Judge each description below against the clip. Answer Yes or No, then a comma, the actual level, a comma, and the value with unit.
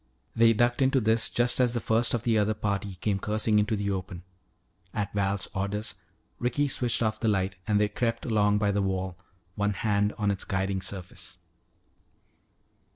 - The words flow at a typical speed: Yes, average, 175 wpm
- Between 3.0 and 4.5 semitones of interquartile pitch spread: No, narrow, 2.5 semitones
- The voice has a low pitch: Yes, low, 105 Hz